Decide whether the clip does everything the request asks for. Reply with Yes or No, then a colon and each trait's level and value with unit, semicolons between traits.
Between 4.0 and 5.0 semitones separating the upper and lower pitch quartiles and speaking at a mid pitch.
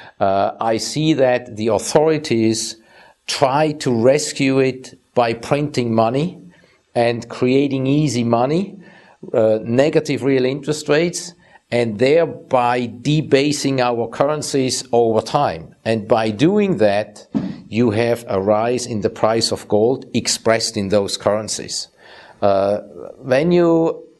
No: average, 4.7 semitones; low, 125 Hz